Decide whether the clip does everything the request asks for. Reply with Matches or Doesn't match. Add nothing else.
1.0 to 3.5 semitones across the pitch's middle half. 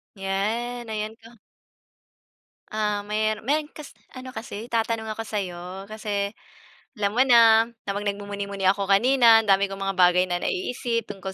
Matches